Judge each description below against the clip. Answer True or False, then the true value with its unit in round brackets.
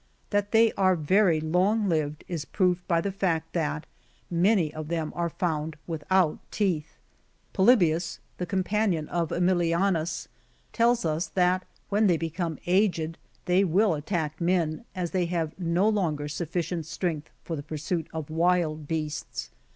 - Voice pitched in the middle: True (170 Hz)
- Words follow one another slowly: False (150 wpm)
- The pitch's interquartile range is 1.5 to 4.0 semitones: True (2.9 semitones)